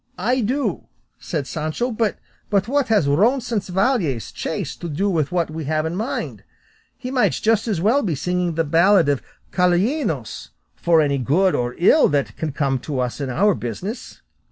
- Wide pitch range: Yes, wide, 6.7 semitones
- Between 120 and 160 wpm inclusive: No, average, 170 wpm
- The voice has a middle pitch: Yes, medium, 175 Hz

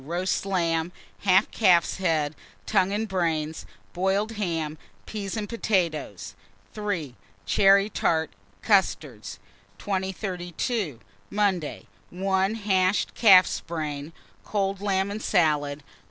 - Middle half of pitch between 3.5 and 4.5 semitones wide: Yes, average, 3.9 semitones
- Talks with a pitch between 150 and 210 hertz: Yes, medium, 185 Hz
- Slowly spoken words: Yes, slow, 100 wpm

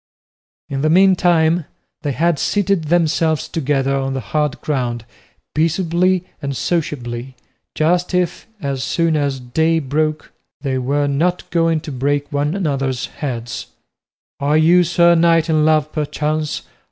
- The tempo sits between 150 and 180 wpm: No, average, 140 wpm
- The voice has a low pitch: No, medium, 155 Hz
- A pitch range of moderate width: Yes, average, 3.2 semitones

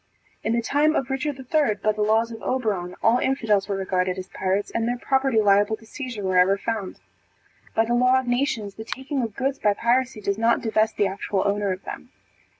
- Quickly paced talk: Yes, fast, 210 wpm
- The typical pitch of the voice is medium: No, high, 225 Hz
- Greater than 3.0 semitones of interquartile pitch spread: Yes, average, 4.1 semitones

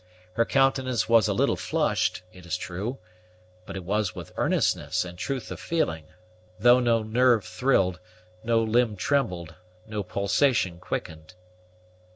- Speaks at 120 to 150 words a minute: Yes, average, 140 wpm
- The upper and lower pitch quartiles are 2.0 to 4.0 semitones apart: No, average, 5.2 semitones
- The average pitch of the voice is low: Yes, low, 110 Hz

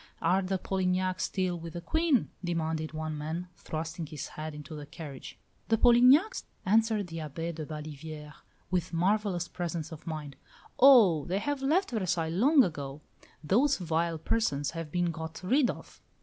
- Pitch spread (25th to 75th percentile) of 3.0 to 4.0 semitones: No, average, 4.4 semitones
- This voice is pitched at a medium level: Yes, medium, 170 Hz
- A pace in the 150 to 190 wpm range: Yes, average, 160 wpm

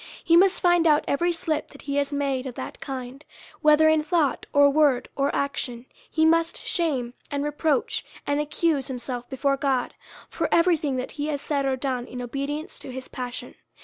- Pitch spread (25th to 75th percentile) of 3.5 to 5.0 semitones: No, average, 3.1 semitones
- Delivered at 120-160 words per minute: No, average, 195 wpm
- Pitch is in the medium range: No, very high, 285 Hz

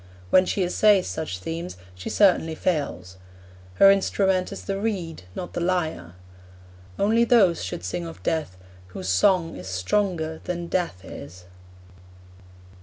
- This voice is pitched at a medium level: Yes, medium, 170 Hz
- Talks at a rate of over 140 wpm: No, slow, 135 wpm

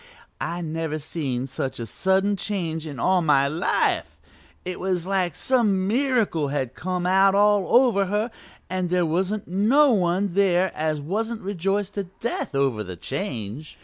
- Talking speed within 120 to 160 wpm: Yes, average, 155 wpm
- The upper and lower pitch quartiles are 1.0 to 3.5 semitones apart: No, average, 4.4 semitones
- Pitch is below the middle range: No, medium, 185 Hz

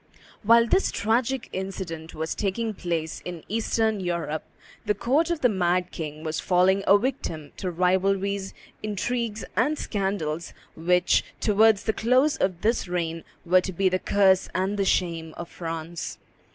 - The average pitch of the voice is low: No, high, 190 Hz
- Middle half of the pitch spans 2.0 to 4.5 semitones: Yes, average, 4.2 semitones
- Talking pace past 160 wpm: No, average, 150 wpm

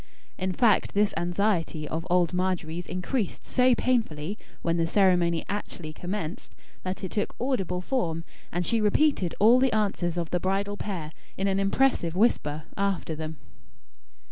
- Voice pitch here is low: No, medium, 185 Hz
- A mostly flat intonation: No, average, 3.7 semitones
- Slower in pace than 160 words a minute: Yes, average, 150 wpm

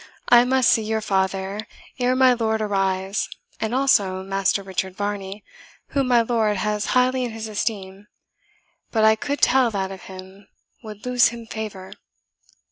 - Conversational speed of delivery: Yes, average, 155 wpm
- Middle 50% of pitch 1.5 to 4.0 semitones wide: Yes, average, 3.6 semitones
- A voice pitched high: Yes, high, 215 Hz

